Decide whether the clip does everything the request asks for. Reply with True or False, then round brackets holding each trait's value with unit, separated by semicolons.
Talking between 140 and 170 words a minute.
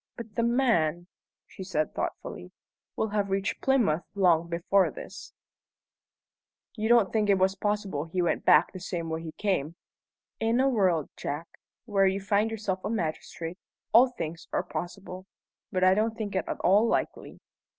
True (160 wpm)